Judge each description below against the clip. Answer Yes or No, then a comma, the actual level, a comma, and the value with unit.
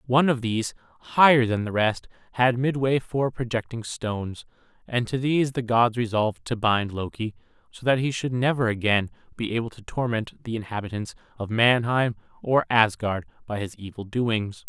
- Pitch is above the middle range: No, low, 115 Hz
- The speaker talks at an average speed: Yes, average, 170 wpm